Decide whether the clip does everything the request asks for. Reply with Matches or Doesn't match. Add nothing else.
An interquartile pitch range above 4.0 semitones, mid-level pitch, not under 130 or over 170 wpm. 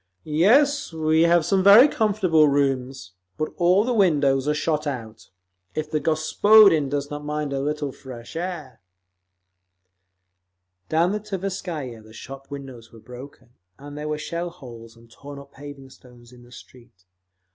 Matches